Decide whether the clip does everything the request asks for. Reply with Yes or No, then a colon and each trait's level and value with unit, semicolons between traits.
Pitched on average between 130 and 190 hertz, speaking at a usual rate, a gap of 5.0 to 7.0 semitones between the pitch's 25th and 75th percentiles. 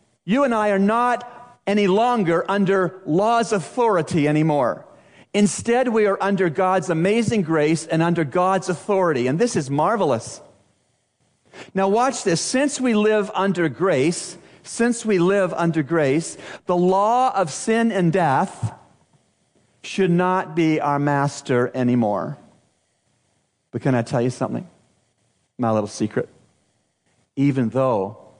No: medium, 185 Hz; slow, 130 wpm; average, 5.3 semitones